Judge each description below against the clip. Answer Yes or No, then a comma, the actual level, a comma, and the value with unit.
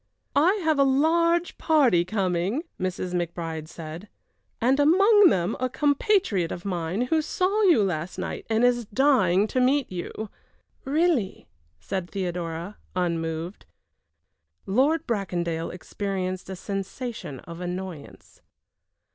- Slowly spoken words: Yes, slow, 120 wpm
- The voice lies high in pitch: Yes, high, 195 Hz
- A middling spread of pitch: No, wide, 8.0 semitones